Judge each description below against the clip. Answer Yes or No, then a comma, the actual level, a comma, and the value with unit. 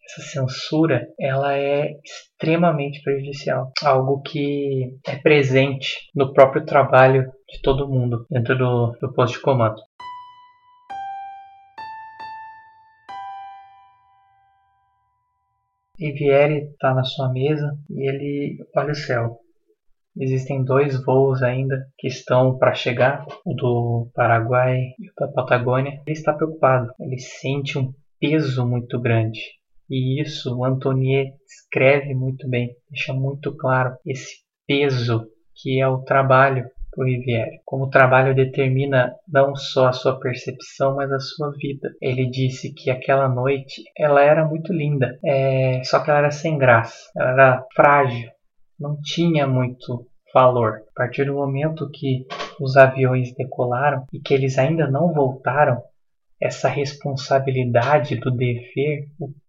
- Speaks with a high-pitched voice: No, low, 135 Hz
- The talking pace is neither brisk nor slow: Yes, average, 130 wpm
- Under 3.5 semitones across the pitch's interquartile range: Yes, narrow, 2.4 semitones